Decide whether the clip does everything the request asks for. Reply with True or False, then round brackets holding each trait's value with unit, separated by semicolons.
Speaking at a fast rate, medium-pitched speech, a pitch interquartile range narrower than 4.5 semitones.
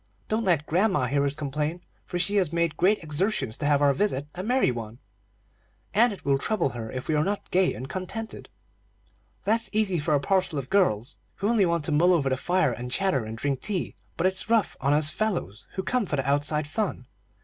False (215 wpm; 165 Hz; 5.6 semitones)